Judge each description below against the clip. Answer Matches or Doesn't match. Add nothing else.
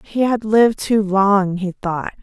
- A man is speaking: Doesn't match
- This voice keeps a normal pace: Matches